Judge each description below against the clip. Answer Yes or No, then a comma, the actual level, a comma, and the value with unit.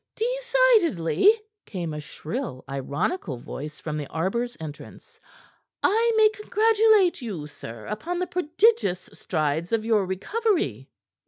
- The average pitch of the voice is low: No, high, 230 Hz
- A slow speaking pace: Yes, slow, 115 wpm